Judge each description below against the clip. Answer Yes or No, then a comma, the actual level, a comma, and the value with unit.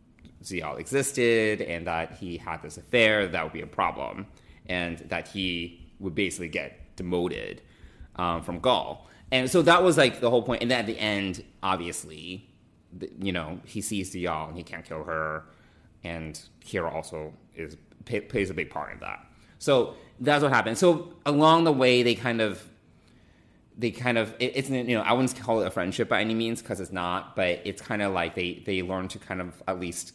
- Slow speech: No, fast, 205 wpm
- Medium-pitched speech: No, very low, 95 Hz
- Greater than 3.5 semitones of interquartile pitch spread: Yes, wide, 5.5 semitones